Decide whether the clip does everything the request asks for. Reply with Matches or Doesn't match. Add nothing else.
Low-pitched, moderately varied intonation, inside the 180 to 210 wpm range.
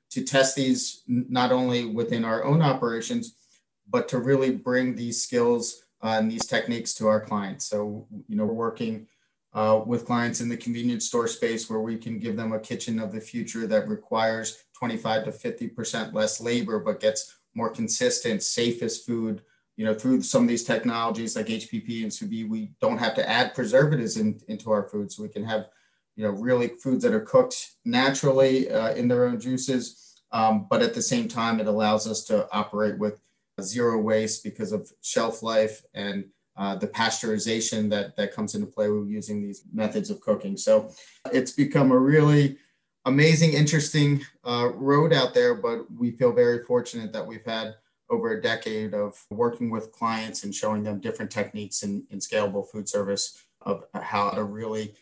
Matches